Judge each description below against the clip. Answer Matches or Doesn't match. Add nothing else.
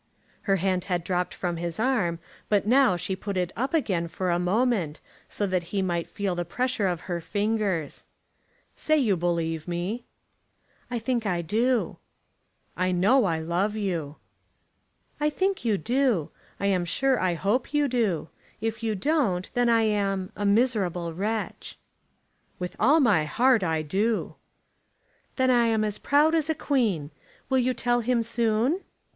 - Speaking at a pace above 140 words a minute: Matches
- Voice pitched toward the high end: Matches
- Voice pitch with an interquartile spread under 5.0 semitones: Doesn't match